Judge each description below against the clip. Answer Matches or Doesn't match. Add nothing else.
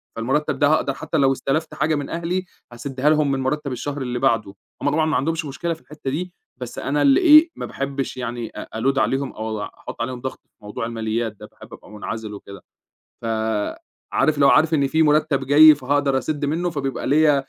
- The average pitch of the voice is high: Doesn't match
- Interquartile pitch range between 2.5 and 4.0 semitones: Matches